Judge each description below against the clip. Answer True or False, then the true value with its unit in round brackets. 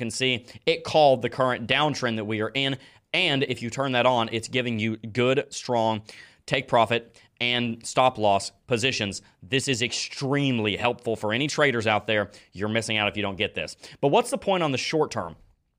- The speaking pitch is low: True (120 Hz)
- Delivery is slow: False (200 wpm)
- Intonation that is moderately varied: True (3.5 semitones)